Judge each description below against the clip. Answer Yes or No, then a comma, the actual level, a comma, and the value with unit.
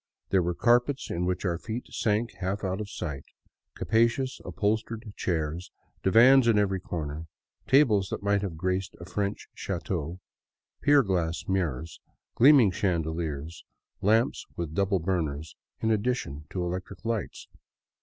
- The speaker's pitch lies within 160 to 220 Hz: No, very low, 95 Hz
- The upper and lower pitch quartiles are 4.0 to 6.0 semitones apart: Yes, average, 4.8 semitones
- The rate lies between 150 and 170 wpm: No, slow, 135 wpm